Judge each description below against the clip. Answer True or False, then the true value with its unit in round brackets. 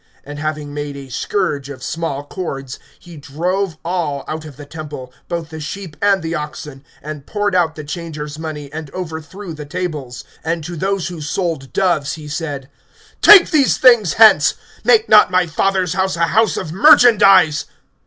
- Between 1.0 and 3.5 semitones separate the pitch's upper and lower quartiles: False (3.9 semitones)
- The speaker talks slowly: False (175 wpm)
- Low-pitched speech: False (160 Hz)